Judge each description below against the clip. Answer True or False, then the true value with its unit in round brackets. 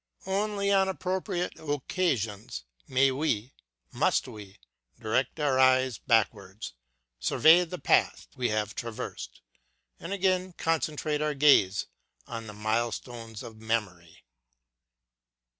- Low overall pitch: True (130 Hz)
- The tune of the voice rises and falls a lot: True (7.1 semitones)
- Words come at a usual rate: False (110 wpm)